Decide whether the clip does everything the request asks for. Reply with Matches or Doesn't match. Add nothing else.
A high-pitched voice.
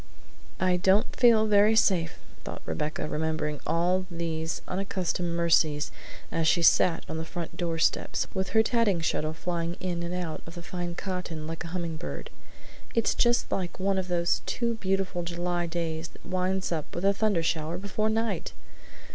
Doesn't match